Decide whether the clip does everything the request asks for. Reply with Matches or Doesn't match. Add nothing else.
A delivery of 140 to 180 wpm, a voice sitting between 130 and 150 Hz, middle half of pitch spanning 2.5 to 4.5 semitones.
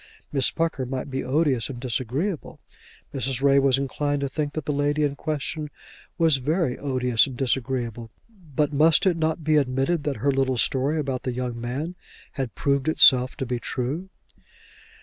Matches